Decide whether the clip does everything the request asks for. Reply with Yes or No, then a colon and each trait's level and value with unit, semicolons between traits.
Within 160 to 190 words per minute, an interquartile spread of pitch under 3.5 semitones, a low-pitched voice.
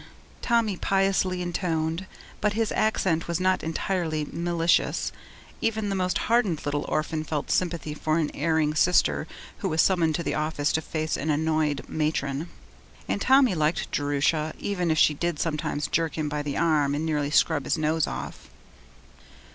No: average, 165 wpm; average, 3.0 semitones; medium, 160 Hz